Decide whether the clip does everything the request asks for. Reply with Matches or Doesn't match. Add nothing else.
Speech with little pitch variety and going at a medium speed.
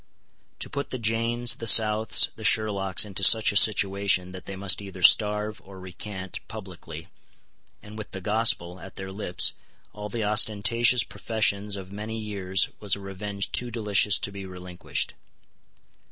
Matches